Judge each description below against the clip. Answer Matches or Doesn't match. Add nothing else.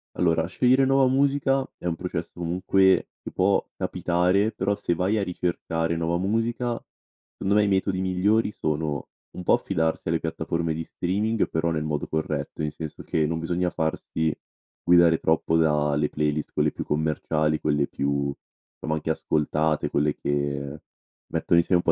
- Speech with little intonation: Doesn't match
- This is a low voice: Matches